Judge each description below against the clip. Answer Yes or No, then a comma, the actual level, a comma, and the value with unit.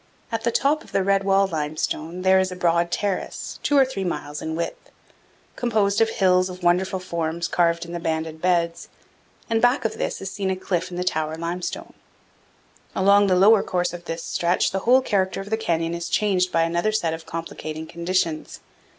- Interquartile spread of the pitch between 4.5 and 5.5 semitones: No, average, 2.8 semitones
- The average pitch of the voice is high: No, medium, 180 Hz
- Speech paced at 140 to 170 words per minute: No, average, 200 wpm